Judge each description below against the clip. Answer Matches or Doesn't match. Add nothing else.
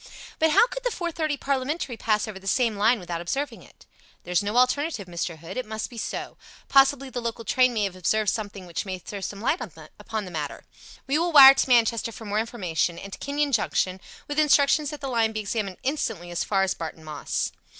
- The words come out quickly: Matches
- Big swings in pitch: Matches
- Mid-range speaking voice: Doesn't match